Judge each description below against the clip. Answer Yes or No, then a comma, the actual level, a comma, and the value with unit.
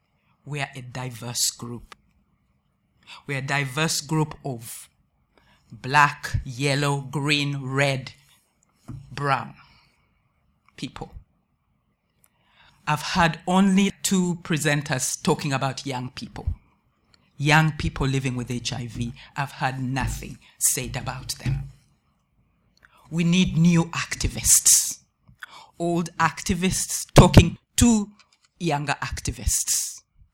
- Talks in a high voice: No, medium, 140 Hz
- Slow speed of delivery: Yes, slow, 90 wpm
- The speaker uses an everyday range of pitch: Yes, average, 3.7 semitones